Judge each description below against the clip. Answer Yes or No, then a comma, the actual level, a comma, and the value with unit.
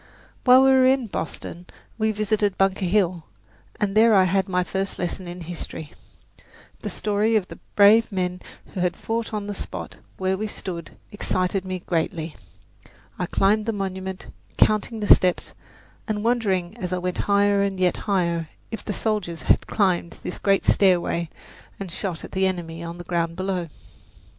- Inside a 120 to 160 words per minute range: No, average, 170 wpm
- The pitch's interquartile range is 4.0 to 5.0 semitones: No, average, 2.8 semitones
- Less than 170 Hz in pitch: No, high, 190 Hz